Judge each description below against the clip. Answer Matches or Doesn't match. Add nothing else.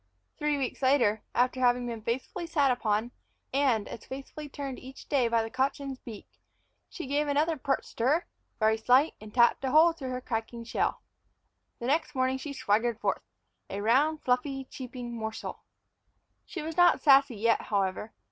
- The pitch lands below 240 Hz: Doesn't match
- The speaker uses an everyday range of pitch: Matches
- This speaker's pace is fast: Doesn't match